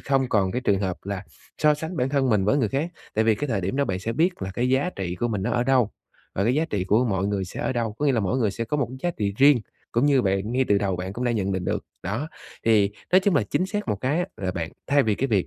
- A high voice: No, low, 115 Hz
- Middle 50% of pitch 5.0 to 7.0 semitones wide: Yes, wide, 5.5 semitones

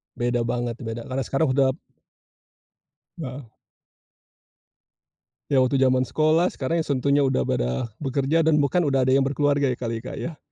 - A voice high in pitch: No, low, 135 Hz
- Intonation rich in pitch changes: No, narrow, 2.5 semitones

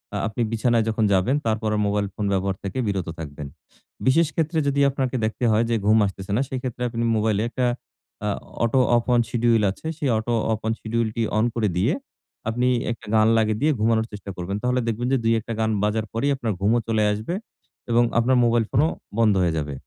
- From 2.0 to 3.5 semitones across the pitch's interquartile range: Yes, narrow, 2.5 semitones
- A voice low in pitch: Yes, low, 110 Hz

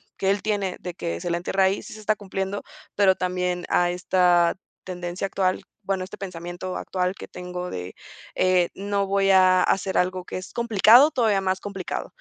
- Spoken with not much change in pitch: Yes, narrow, 1.5 semitones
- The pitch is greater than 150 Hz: Yes, medium, 185 Hz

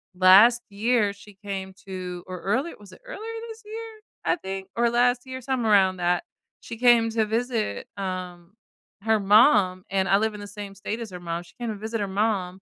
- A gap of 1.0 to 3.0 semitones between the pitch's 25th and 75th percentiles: No, average, 3.9 semitones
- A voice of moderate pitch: No, high, 205 Hz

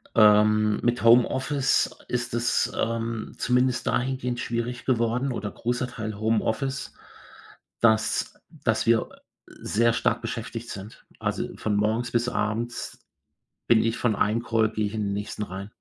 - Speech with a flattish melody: Yes, narrow, 2.1 semitones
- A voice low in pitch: Yes, low, 115 Hz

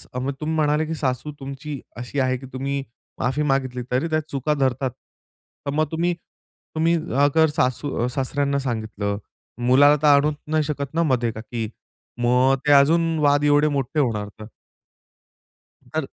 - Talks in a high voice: No, medium, 140 Hz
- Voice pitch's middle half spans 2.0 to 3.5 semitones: Yes, average, 2.9 semitones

